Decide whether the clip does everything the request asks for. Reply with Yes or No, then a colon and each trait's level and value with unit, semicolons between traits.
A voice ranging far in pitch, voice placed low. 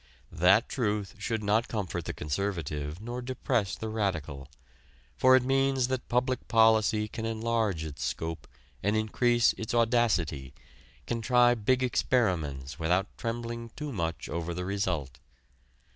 Yes: wide, 5.7 semitones; low, 110 Hz